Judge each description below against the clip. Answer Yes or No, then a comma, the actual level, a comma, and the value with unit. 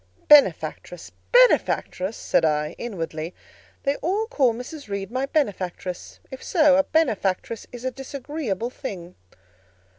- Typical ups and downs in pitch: No, wide, 7.3 semitones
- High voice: Yes, high, 245 Hz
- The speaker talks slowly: Yes, slow, 120 wpm